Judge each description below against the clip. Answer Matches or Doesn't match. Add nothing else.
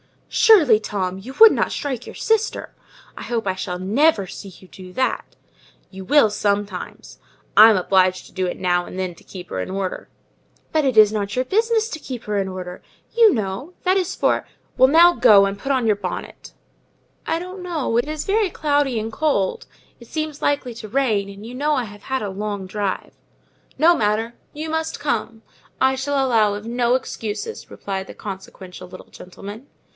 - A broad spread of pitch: Matches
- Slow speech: Doesn't match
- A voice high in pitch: Matches